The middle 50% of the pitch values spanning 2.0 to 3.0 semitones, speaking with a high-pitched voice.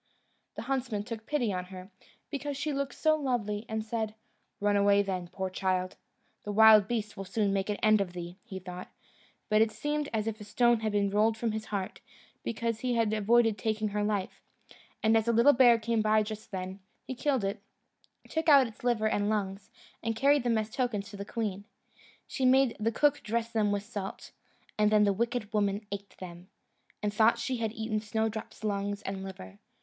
Yes: narrow, 2.5 semitones; high, 215 Hz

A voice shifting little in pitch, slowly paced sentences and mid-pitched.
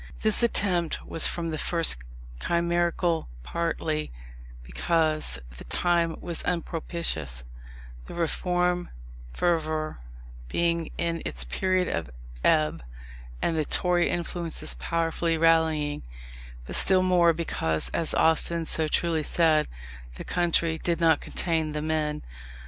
Yes: narrow, 1.8 semitones; slow, 115 wpm; medium, 165 Hz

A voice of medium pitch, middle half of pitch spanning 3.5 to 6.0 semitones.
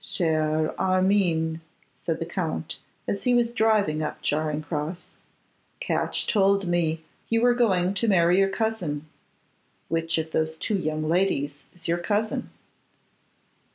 Yes: medium, 175 Hz; average, 4.1 semitones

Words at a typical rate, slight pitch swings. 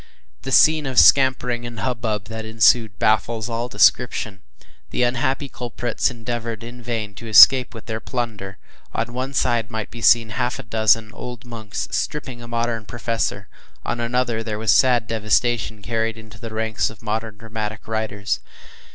Yes: average, 160 wpm; narrow, 1.7 semitones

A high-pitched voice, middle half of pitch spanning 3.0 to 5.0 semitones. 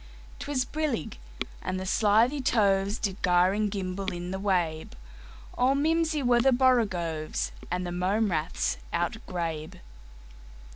No: high, 195 Hz; wide, 5.6 semitones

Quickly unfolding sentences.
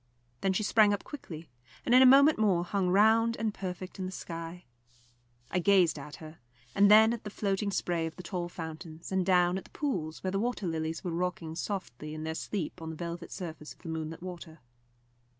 Yes: fast, 210 wpm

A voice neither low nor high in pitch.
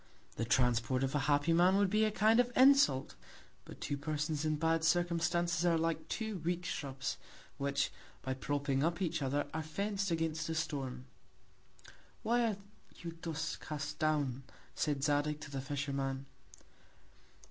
Yes: medium, 155 Hz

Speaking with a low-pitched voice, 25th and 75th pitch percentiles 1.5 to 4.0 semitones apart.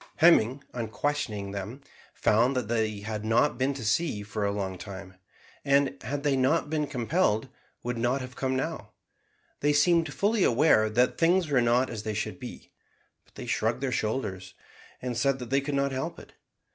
No: low, 125 Hz; average, 4.5 semitones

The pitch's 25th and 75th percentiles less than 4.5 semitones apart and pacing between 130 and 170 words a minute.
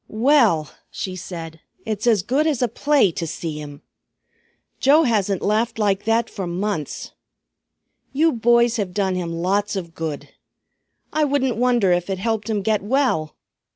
No: average, 5.0 semitones; average, 155 wpm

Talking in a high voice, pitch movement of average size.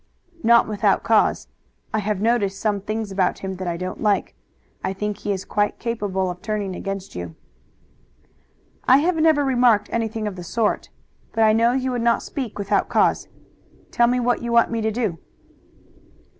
Yes: high, 215 Hz; average, 3.3 semitones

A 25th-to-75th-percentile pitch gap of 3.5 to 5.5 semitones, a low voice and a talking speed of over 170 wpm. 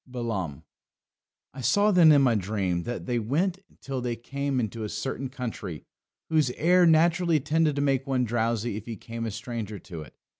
Yes: average, 4.7 semitones; low, 125 Hz; average, 185 wpm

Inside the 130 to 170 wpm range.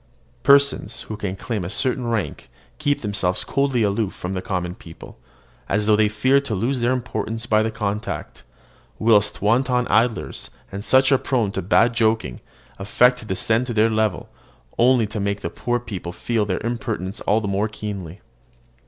No: average, 180 wpm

